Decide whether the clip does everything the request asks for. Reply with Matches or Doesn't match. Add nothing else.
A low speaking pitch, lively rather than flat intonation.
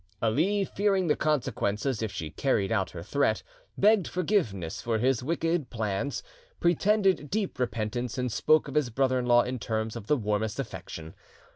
Matches